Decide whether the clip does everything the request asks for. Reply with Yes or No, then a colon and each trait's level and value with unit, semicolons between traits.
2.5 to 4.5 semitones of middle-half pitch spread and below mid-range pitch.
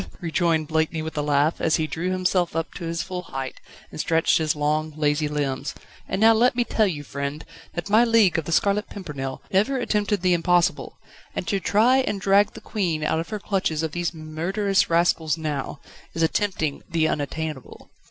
No: average, 4.2 semitones; medium, 165 Hz